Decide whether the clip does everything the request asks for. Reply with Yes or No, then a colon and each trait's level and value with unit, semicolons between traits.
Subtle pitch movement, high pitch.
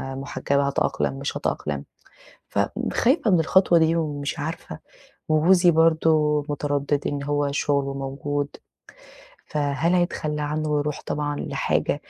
No: narrow, 2.3 semitones; medium, 145 Hz